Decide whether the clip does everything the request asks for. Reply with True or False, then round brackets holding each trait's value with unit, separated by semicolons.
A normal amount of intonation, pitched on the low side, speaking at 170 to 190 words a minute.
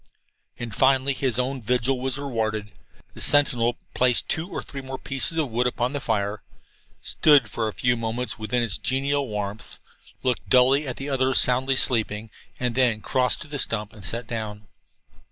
True (3.1 semitones; 125 Hz; 180 wpm)